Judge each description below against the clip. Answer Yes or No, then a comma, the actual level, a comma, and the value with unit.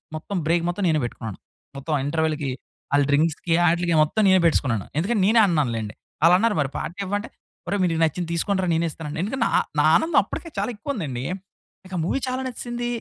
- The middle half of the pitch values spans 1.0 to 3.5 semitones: No, average, 5.1 semitones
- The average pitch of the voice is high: No, medium, 170 Hz